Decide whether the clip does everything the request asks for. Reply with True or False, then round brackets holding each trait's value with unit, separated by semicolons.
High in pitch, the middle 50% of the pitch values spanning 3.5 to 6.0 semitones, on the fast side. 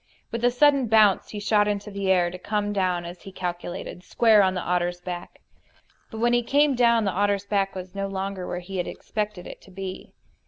False (195 Hz; 2.9 semitones; 220 wpm)